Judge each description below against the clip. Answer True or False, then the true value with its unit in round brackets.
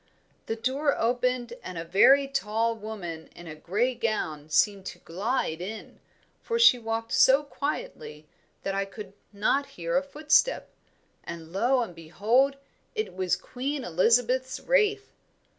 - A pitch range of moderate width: False (6.3 semitones)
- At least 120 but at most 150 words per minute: True (140 wpm)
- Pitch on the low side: False (225 Hz)